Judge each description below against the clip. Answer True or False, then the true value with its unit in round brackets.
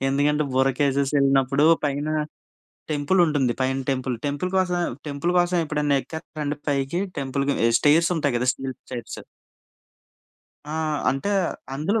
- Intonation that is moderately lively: False (2.3 semitones)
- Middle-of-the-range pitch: True (145 Hz)